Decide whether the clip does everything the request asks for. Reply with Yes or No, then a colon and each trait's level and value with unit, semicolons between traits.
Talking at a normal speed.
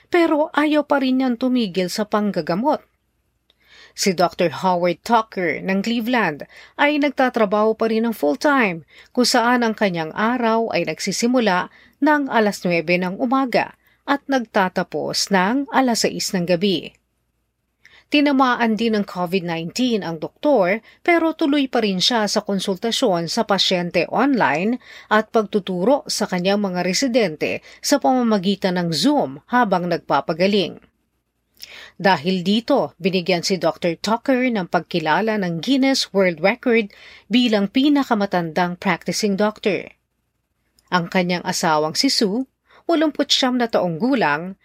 Yes: average, 125 wpm